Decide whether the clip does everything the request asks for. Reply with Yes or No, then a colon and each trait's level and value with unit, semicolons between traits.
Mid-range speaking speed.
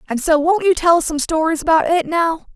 No: fast, 260 wpm